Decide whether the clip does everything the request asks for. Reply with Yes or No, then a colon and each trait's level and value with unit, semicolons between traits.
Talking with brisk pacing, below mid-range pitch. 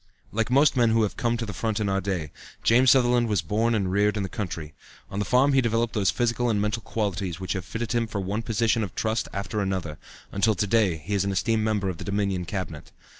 Yes: fast, 245 wpm; low, 105 Hz